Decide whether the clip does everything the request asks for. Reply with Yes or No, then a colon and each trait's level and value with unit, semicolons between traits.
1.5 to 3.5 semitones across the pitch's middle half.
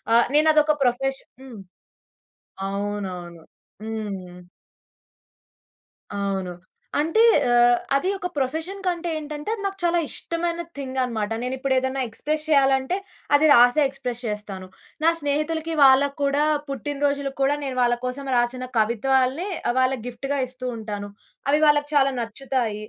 No: average, 3.9 semitones